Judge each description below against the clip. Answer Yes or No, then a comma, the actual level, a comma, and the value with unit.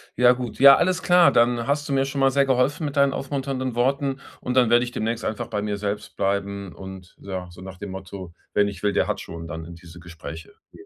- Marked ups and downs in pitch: Yes, wide, 6.0 semitones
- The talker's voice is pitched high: No, low, 115 Hz